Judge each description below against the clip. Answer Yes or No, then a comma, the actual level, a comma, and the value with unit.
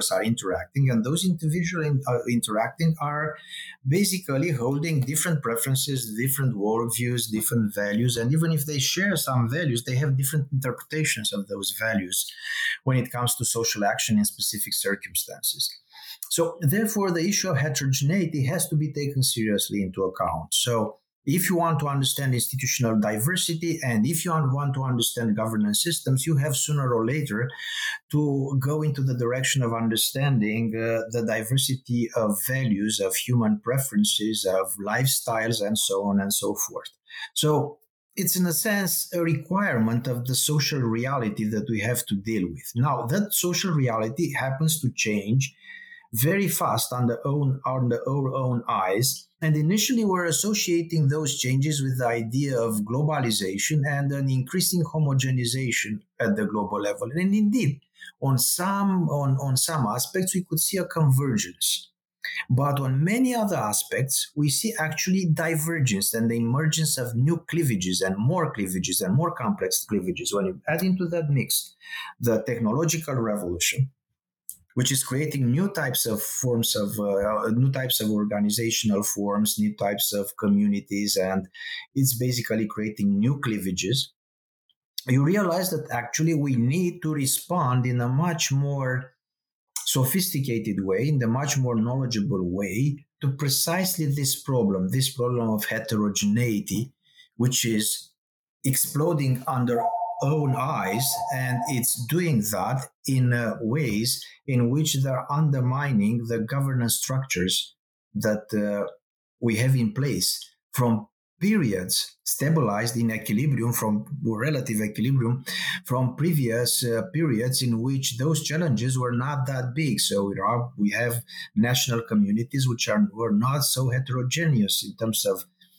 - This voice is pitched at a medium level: No, low, 130 Hz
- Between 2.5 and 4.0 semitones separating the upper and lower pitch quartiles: No, average, 5.2 semitones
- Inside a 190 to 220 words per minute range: No, average, 145 wpm